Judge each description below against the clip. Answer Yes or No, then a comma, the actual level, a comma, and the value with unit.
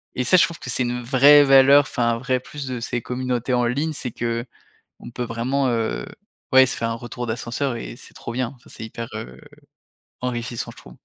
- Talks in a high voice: No, low, 125 Hz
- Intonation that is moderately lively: No, narrow, 2.0 semitones